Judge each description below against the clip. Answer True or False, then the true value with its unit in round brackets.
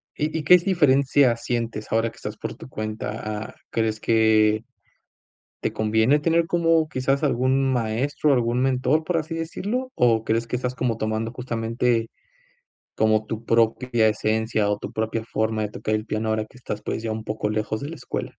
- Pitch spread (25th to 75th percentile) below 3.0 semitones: False (3.7 semitones)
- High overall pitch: False (115 Hz)